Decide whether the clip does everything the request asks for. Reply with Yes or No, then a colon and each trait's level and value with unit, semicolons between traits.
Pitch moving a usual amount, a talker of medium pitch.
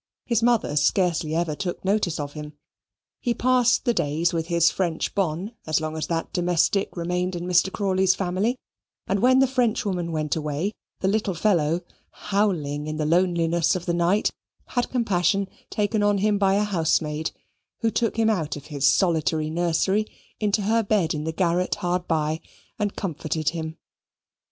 Yes: average, 4.4 semitones; medium, 180 Hz